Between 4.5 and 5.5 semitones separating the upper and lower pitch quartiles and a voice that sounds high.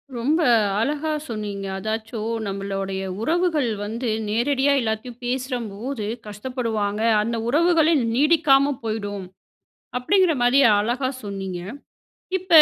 Yes: average, 5.1 semitones; high, 235 Hz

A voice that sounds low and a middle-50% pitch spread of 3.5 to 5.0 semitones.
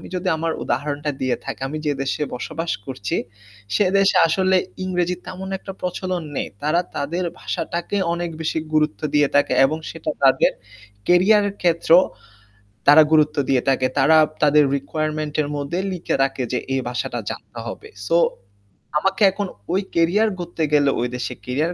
No: medium, 160 Hz; average, 3.9 semitones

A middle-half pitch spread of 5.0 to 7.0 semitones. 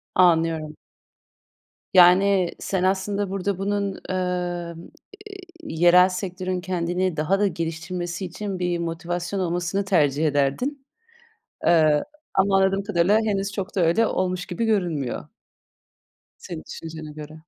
No: average, 2.7 semitones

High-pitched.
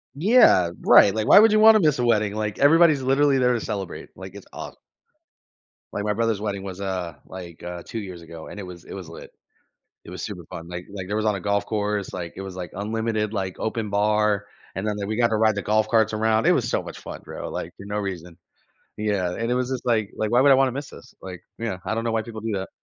No: low, 105 Hz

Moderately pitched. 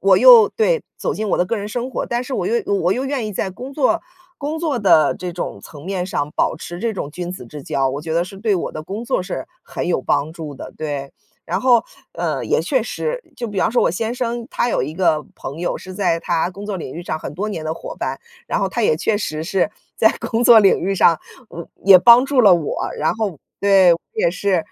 No: high, 195 Hz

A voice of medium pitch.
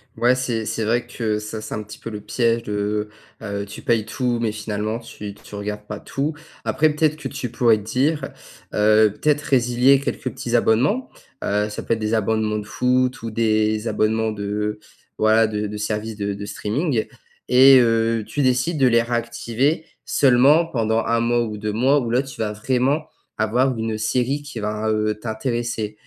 No: low, 115 Hz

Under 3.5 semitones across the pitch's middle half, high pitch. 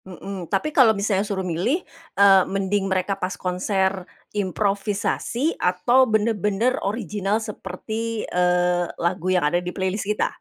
Yes: average, 2.7 semitones; high, 195 Hz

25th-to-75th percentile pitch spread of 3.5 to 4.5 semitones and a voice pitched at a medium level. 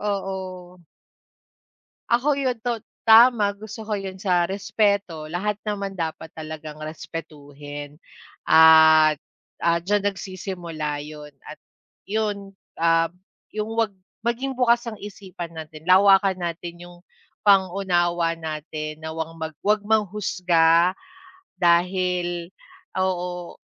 Yes: average, 4.1 semitones; medium, 180 Hz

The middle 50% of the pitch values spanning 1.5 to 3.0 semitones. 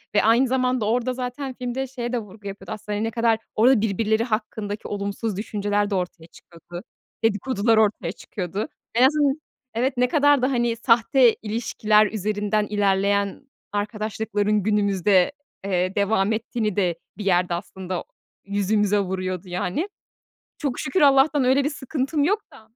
No: average, 3.7 semitones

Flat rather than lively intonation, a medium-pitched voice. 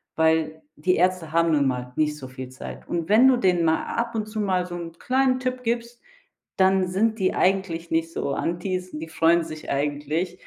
No: average, 3.6 semitones; medium, 175 Hz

